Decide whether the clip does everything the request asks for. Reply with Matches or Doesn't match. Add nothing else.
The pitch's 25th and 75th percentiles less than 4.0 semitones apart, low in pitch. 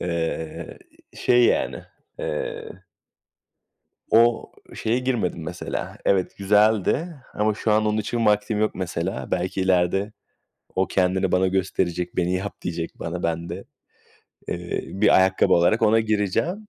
Matches